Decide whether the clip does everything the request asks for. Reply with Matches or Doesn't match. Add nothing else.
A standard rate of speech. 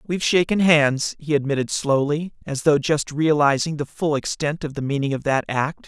Matches